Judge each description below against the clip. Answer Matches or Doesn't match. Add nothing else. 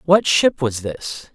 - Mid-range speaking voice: Matches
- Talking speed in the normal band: Matches